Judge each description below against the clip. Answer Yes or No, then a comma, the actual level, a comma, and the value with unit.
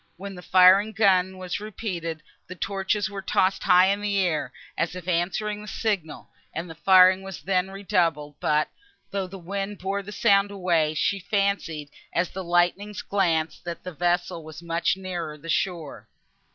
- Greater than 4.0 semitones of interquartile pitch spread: No, average, 2.7 semitones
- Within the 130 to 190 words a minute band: Yes, average, 175 wpm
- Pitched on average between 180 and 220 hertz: Yes, medium, 185 Hz